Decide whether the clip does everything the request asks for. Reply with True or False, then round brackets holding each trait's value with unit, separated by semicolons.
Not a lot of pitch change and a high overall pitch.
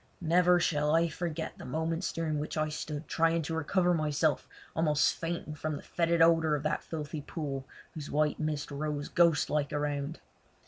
False (1.8 semitones; 155 Hz)